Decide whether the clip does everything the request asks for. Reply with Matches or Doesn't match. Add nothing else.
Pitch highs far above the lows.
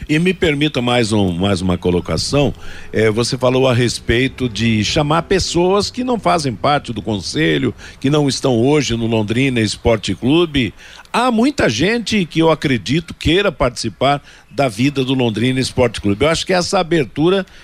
Matches